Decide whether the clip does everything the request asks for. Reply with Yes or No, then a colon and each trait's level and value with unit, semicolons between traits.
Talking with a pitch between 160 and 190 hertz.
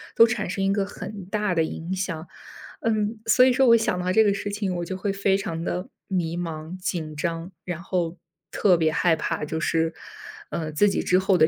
Yes: medium, 185 Hz